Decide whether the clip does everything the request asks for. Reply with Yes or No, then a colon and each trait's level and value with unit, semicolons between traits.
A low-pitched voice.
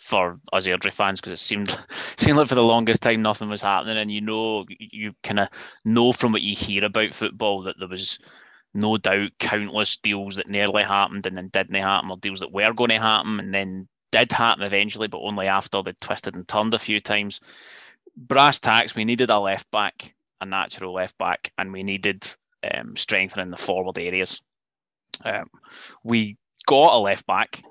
Yes: low, 105 Hz